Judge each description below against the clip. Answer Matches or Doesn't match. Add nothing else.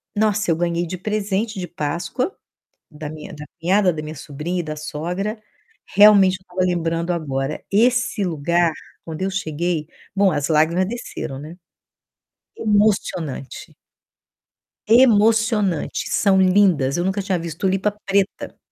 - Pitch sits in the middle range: Matches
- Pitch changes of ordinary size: Matches